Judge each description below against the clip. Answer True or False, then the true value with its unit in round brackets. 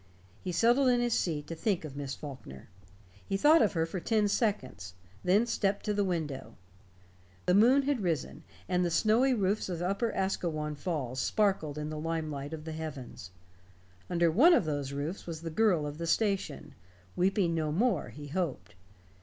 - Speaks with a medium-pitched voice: True (170 Hz)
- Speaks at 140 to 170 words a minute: False (180 wpm)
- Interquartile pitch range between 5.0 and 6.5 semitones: True (5.4 semitones)